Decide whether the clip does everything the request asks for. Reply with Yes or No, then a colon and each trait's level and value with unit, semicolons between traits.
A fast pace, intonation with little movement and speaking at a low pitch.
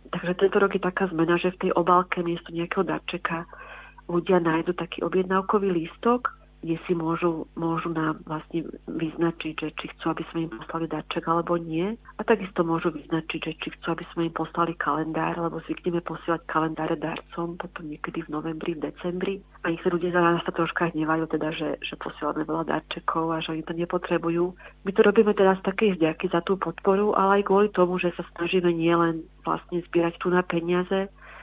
No: fast, 190 wpm; narrow, 2.1 semitones; medium, 170 Hz